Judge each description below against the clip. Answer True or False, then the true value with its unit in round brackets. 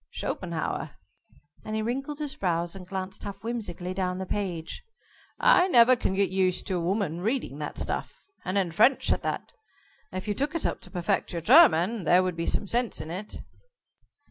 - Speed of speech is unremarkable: True (190 wpm)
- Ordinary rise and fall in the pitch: True (4.6 semitones)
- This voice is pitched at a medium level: False (195 Hz)